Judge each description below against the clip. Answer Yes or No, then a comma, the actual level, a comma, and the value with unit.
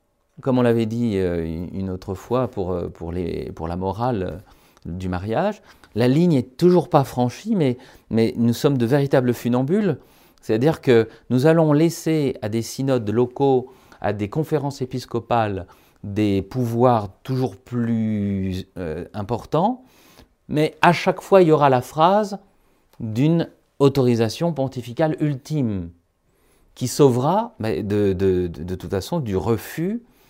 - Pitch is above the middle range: No, low, 125 Hz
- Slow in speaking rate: Yes, slow, 125 wpm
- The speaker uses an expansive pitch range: Yes, wide, 7.0 semitones